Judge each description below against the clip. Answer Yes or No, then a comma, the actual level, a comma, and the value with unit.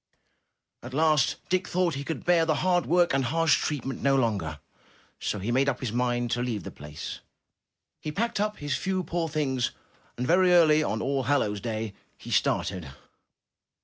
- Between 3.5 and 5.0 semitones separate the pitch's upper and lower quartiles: No, wide, 5.6 semitones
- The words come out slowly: No, average, 180 wpm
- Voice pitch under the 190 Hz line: Yes, medium, 140 Hz